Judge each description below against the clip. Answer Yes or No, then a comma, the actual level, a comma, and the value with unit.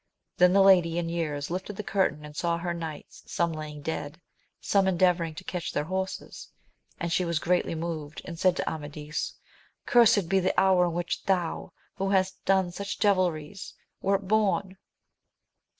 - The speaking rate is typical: Yes, average, 165 wpm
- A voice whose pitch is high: No, medium, 175 Hz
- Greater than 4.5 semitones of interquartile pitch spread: No, average, 2.7 semitones